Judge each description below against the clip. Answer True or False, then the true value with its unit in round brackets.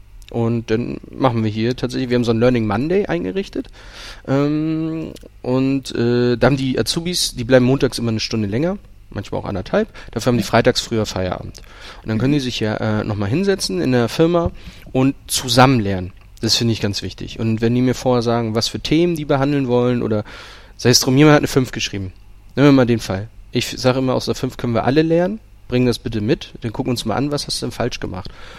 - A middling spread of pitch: True (3.6 semitones)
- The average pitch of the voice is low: True (120 Hz)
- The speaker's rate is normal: False (230 wpm)